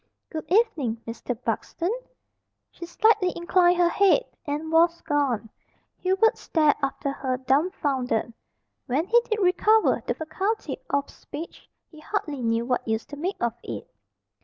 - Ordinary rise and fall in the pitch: No, wide, 5.8 semitones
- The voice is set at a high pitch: Yes, very high, 315 Hz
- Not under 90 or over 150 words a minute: Yes, average, 140 wpm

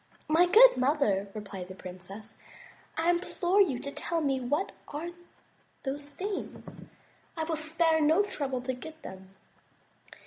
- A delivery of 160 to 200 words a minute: No, average, 140 wpm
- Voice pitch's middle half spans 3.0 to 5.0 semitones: No, wide, 5.6 semitones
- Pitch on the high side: Yes, very high, 295 Hz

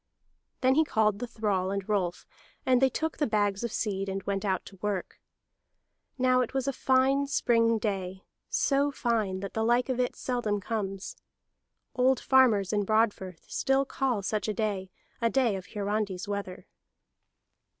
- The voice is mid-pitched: No, high, 215 Hz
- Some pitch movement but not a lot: Yes, average, 4.3 semitones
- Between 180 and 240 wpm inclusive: No, average, 165 wpm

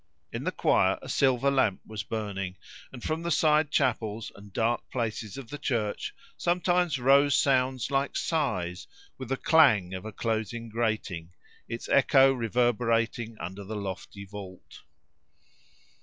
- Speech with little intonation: No, average, 4.8 semitones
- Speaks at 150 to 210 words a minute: No, average, 140 wpm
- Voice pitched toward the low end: Yes, low, 115 Hz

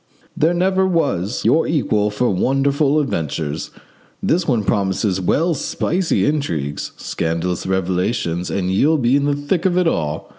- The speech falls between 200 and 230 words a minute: No, average, 145 wpm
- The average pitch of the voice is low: Yes, low, 120 Hz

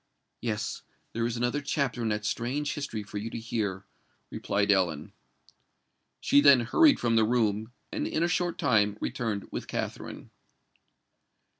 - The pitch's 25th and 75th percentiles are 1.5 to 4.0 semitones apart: Yes, average, 3.6 semitones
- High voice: No, low, 115 Hz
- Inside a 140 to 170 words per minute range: Yes, average, 145 wpm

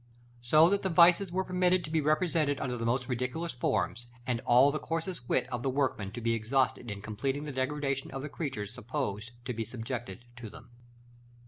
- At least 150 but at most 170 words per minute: No, average, 200 wpm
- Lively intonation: No, average, 4.3 semitones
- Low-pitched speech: Yes, low, 130 Hz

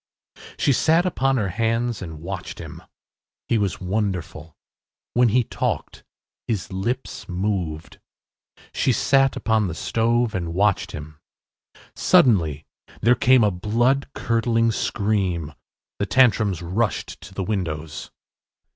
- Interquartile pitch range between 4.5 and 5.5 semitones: Yes, average, 4.8 semitones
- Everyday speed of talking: No, slow, 120 wpm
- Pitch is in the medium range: No, low, 105 Hz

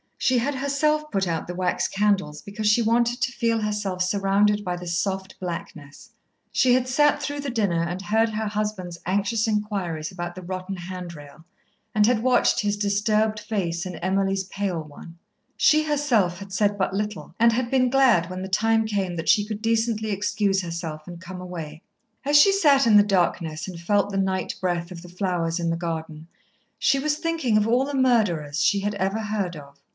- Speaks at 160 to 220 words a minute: Yes, average, 195 wpm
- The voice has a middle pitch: No, high, 200 Hz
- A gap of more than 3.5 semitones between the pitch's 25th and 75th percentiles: Yes, average, 4.2 semitones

